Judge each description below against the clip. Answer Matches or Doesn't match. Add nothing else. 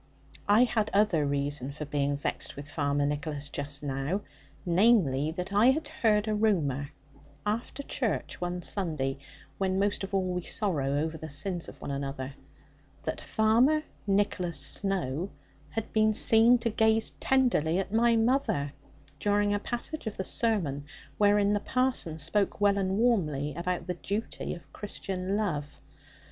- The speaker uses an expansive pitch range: Matches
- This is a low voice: Doesn't match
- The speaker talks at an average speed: Matches